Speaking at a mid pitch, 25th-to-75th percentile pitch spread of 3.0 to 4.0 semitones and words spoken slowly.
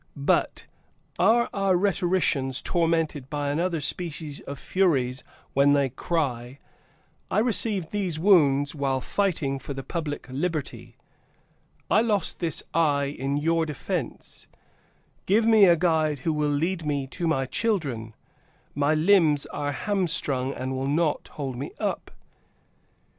No: medium, 150 Hz; average, 4.4 semitones; slow, 130 wpm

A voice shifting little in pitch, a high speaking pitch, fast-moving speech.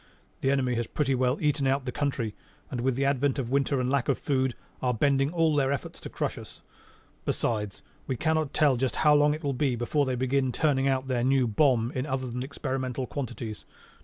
No: narrow, 2.0 semitones; low, 135 Hz; fast, 215 wpm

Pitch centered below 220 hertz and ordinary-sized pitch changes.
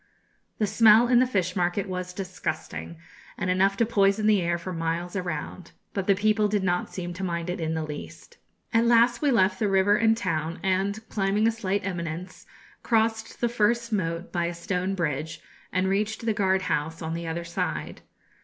Yes: high, 190 Hz; average, 3.8 semitones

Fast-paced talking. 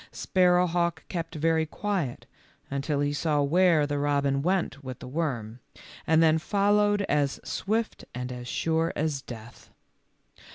No: slow, 135 wpm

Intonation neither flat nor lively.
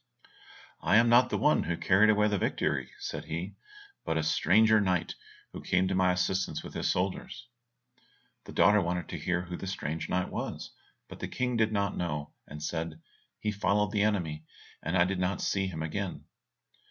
Yes: average, 3.1 semitones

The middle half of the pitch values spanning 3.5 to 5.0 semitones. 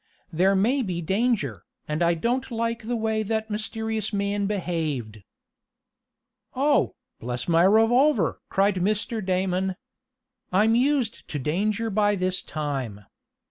Yes: average, 4.6 semitones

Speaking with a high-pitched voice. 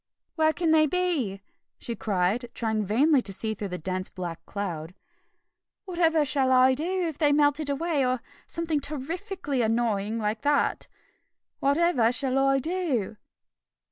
Yes: very high, 270 Hz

